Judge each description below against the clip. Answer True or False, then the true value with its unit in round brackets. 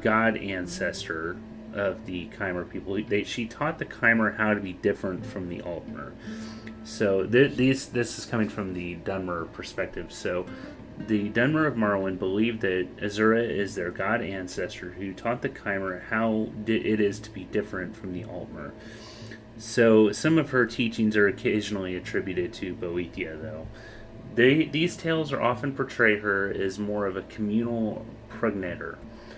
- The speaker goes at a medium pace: True (160 wpm)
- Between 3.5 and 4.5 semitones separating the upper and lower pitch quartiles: False (3.0 semitones)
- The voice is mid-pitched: False (110 Hz)